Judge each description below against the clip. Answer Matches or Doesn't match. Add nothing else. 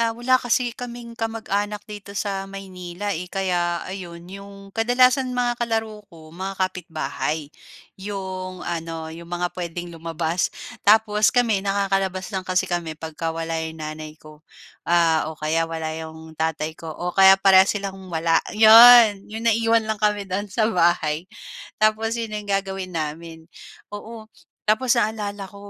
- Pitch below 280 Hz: Matches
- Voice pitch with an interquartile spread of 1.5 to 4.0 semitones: Doesn't match